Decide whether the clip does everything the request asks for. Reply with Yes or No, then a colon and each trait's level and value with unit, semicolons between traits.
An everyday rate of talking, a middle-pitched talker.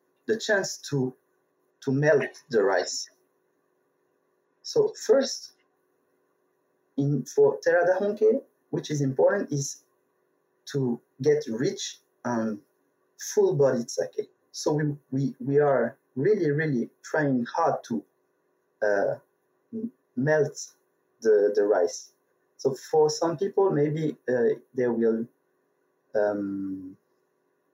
No: slow, 100 wpm; medium, 150 Hz